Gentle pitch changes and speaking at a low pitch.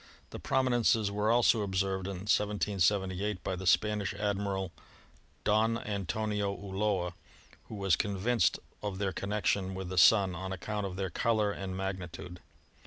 Yes: narrow, 1.8 semitones; low, 100 Hz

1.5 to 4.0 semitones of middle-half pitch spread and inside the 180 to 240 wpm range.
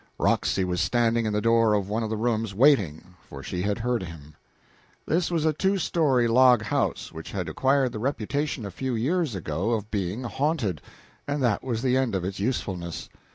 No: average, 5.3 semitones; average, 200 wpm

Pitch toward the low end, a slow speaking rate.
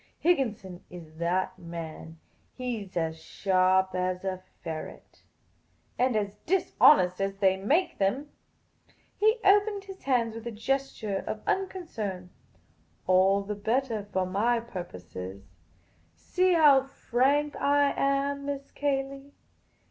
No: high, 220 Hz; slow, 125 wpm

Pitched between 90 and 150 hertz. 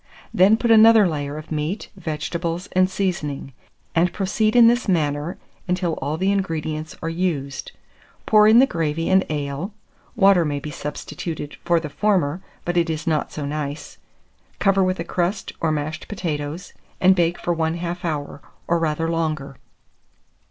No: medium, 165 Hz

